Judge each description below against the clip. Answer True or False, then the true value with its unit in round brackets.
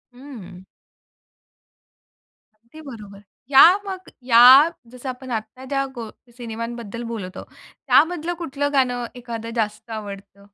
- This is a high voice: True (235 Hz)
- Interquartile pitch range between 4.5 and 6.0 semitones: False (3.7 semitones)